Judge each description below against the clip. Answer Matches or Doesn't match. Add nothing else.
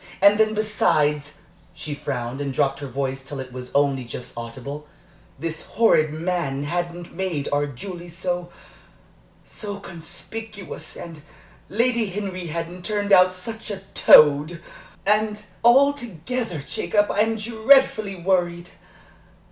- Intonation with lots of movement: Matches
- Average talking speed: Doesn't match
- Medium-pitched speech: Matches